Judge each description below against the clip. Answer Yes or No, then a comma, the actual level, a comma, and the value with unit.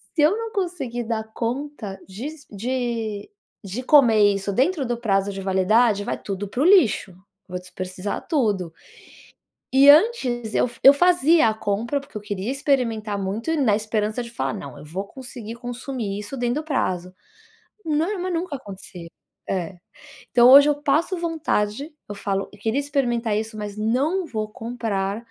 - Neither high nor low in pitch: No, high, 235 Hz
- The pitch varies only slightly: No, wide, 5.5 semitones